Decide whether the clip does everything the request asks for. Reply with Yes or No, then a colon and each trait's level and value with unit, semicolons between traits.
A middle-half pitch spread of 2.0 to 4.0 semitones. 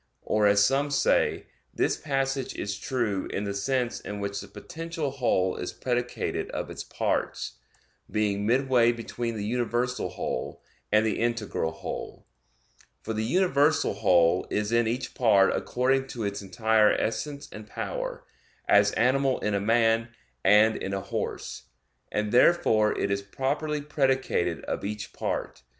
No: average, 4.4 semitones